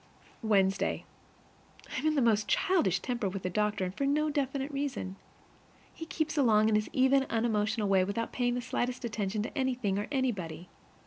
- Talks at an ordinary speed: Yes, average, 180 wpm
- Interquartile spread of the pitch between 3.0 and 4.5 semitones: No, average, 4.9 semitones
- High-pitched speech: Yes, high, 230 Hz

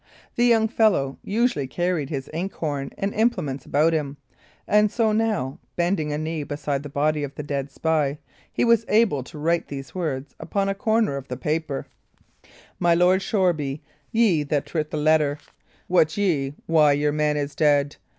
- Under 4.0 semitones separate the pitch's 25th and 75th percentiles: No, average, 5.1 semitones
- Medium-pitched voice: Yes, medium, 155 Hz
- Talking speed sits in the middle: Yes, average, 180 wpm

